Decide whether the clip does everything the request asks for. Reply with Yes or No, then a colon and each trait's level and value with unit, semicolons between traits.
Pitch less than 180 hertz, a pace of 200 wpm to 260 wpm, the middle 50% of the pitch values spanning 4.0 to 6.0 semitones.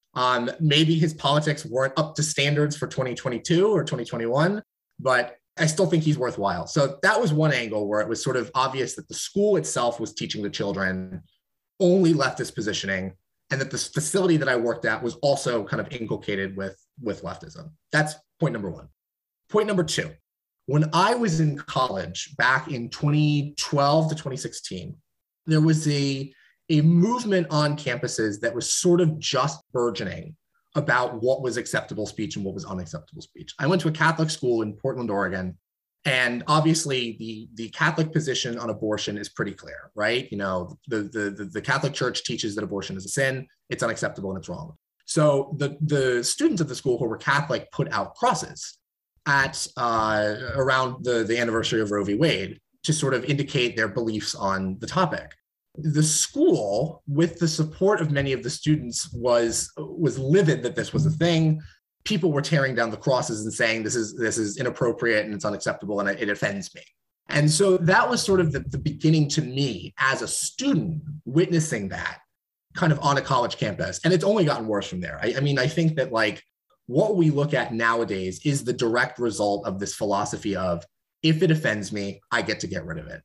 No: medium, 140 Hz; average, 190 wpm; wide, 5.4 semitones